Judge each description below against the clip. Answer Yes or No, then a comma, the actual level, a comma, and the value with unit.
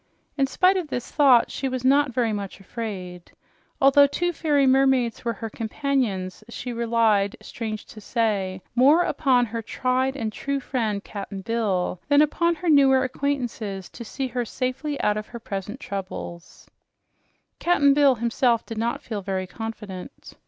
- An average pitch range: Yes, average, 4.5 semitones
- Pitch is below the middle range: No, high, 235 Hz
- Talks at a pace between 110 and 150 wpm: No, average, 160 wpm